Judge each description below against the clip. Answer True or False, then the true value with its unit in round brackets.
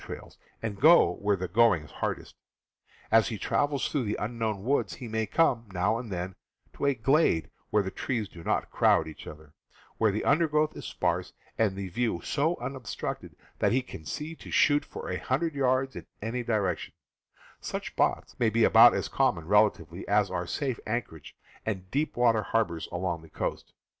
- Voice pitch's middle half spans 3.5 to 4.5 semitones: False (5.6 semitones)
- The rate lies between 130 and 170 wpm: False (190 wpm)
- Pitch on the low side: True (110 Hz)